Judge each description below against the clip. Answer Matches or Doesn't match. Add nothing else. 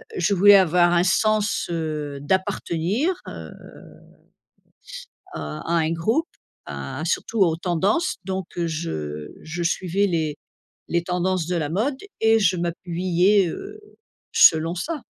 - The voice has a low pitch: Doesn't match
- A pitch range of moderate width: Matches